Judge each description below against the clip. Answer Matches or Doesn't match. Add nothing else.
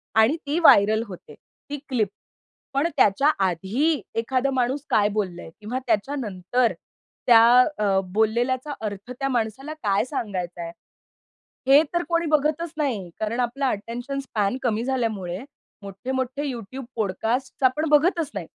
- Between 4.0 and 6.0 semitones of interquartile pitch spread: Matches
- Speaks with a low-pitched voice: Doesn't match